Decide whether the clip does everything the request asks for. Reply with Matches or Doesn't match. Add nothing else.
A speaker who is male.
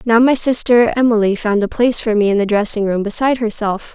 Doesn't match